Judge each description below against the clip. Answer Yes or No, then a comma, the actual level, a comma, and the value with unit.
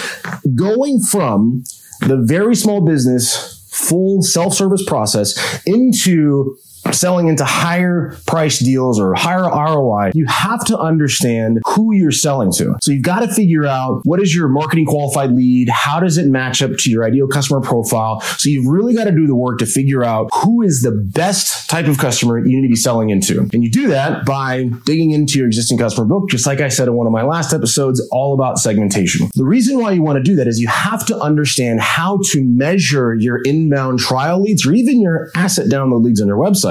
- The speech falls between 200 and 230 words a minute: Yes, fast, 205 wpm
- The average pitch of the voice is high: No, medium, 140 Hz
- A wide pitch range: Yes, wide, 6.2 semitones